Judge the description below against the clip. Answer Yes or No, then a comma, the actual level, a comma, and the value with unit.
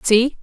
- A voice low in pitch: No, high, 235 Hz